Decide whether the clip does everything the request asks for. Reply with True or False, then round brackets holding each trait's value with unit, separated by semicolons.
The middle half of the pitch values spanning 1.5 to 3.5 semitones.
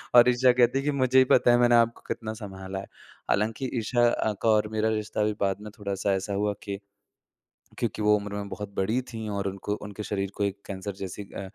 True (2.7 semitones)